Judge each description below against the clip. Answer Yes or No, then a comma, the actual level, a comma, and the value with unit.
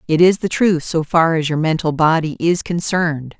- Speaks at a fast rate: Yes, fast, 210 wpm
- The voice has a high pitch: No, medium, 165 Hz